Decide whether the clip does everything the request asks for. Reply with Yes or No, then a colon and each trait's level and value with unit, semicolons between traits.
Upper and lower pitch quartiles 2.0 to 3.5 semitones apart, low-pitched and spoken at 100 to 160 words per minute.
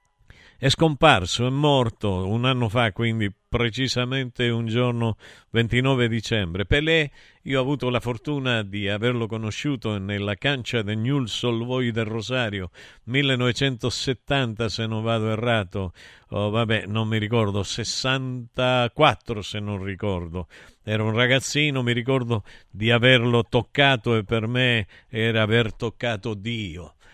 Yes: average, 2.8 semitones; low, 115 Hz; average, 130 wpm